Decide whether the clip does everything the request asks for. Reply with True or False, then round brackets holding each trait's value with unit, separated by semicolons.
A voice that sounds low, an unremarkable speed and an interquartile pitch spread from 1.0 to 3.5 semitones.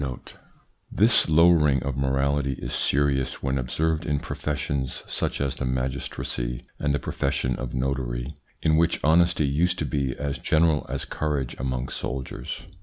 True (70 Hz; 150 wpm; 2.6 semitones)